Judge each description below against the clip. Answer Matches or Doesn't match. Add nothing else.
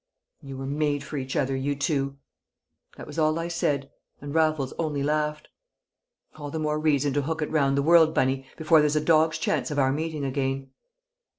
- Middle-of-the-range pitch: Matches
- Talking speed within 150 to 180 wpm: Doesn't match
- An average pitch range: Doesn't match